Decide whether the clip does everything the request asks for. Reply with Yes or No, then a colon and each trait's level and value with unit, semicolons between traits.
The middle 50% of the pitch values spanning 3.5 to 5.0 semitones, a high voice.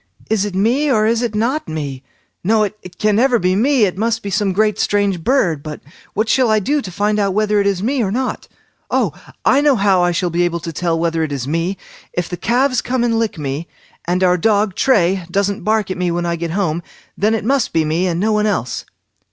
Yes: average, 4.1 semitones; high, 200 Hz